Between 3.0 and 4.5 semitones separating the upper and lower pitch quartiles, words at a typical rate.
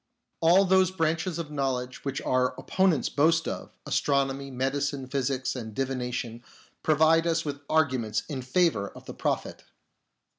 Yes: average, 4.1 semitones; average, 150 wpm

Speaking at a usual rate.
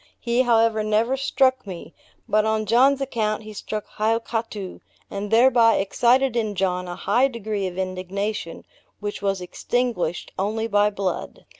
Yes: average, 145 wpm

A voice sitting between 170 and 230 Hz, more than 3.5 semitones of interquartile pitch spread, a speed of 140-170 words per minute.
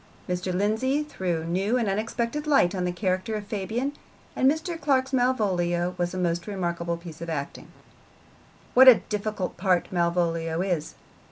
Yes: high, 190 Hz; average, 5.2 semitones; average, 155 wpm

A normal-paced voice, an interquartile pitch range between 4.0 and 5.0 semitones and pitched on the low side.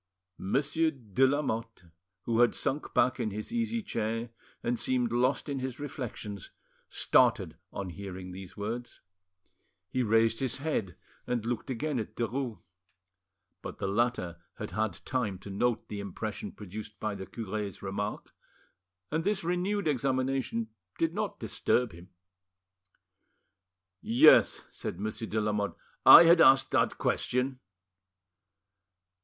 No: slow, 130 wpm; average, 4.3 semitones; low, 115 Hz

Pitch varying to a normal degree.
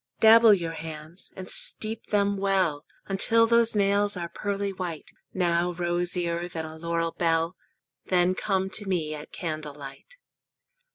Yes: average, 3.3 semitones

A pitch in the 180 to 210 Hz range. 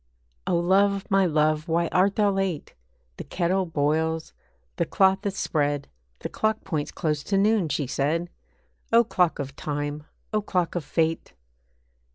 No: medium, 170 Hz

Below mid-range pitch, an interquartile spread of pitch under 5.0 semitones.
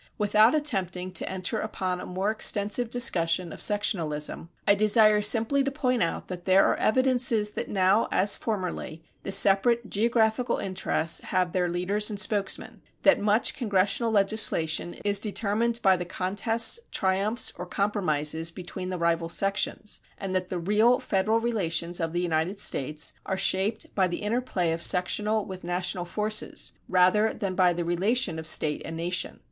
No: high, 195 Hz; average, 3.4 semitones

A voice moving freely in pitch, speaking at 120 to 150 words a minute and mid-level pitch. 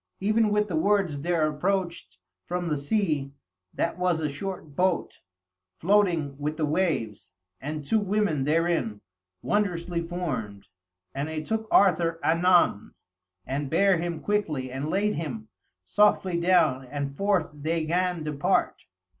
No: average, 4.2 semitones; slow, 135 wpm; medium, 165 Hz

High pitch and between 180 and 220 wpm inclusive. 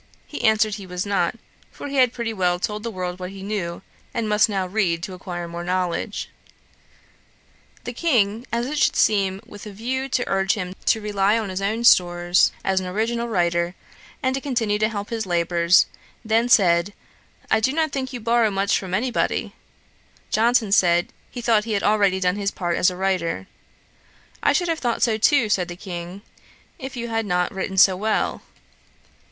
Yes: high, 205 Hz; average, 190 wpm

